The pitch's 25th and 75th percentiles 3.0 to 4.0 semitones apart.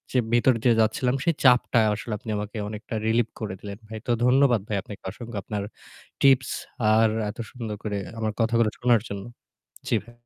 No: narrow, 2.4 semitones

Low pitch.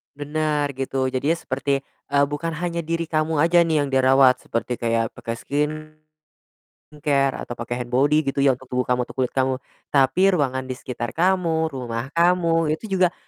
No: medium, 145 Hz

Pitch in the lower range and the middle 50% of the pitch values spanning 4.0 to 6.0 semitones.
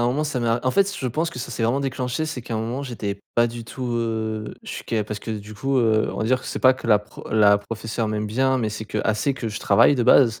No: low, 115 Hz; average, 3.0 semitones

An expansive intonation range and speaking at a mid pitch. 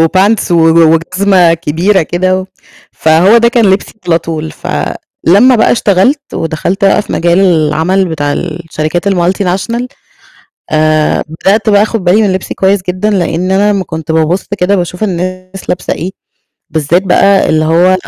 No: average, 3.3 semitones; medium, 180 Hz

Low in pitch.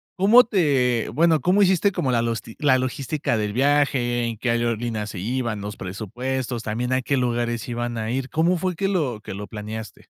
Yes: low, 125 Hz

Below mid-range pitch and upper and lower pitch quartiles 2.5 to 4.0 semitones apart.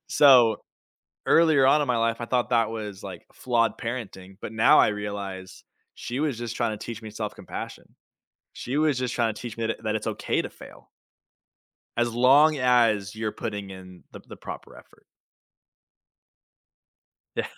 Yes: low, 115 Hz; average, 2.9 semitones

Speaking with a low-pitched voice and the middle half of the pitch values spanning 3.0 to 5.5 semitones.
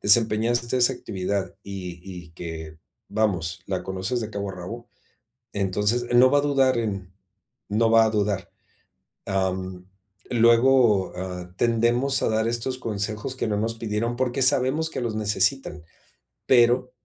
Yes: low, 110 Hz; average, 4.2 semitones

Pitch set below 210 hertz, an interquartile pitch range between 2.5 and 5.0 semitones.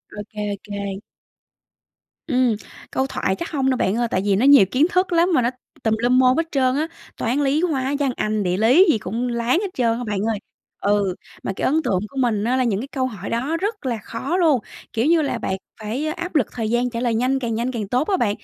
No: very high, 250 Hz; average, 4.3 semitones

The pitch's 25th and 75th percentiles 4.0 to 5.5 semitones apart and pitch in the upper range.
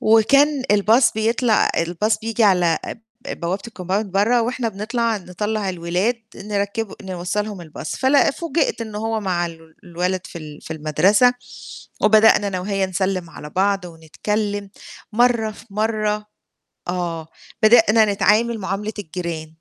No: average, 3.6 semitones; high, 205 Hz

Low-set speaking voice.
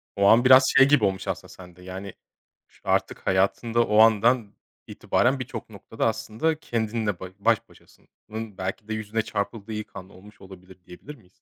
Yes: low, 110 Hz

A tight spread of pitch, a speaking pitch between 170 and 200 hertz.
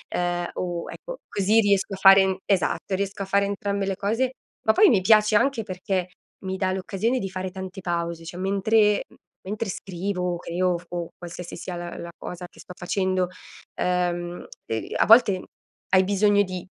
Yes: narrow, 2.1 semitones; high, 190 Hz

